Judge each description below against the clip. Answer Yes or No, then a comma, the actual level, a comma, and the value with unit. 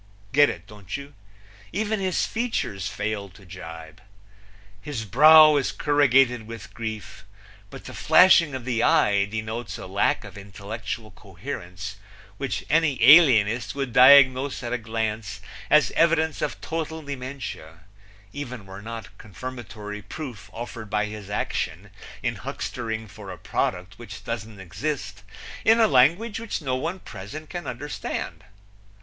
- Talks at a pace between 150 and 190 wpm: No, average, 140 wpm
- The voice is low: Yes, low, 115 Hz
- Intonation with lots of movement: Yes, wide, 5.8 semitones